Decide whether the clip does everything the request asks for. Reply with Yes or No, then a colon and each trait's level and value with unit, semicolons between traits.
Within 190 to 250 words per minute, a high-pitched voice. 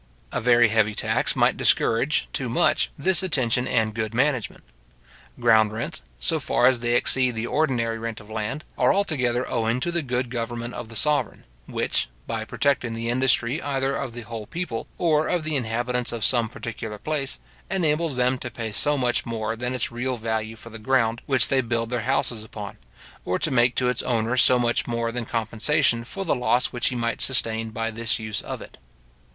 No: average, 195 wpm; low, 120 Hz